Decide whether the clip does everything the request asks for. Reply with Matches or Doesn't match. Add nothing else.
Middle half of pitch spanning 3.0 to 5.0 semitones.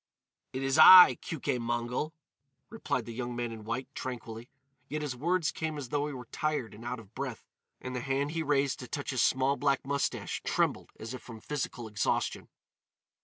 Matches